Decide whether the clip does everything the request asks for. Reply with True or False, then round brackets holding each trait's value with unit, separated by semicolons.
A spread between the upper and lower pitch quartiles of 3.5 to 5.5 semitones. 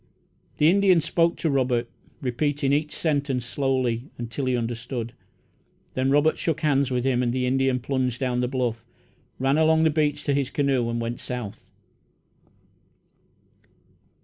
False (3.0 semitones)